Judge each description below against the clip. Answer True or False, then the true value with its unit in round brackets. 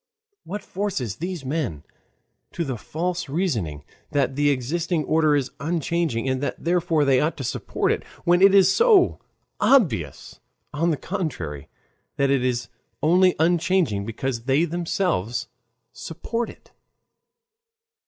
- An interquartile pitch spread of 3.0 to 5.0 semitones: False (5.4 semitones)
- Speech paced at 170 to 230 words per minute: False (135 wpm)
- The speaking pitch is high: False (155 Hz)